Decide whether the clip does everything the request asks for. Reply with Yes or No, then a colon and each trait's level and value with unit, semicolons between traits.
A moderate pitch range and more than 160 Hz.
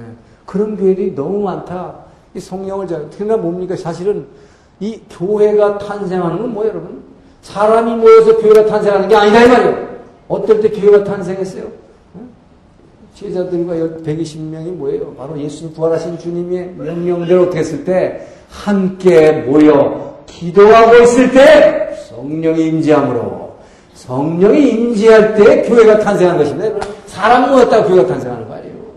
Yes: average, 4.8 semitones; high, 190 Hz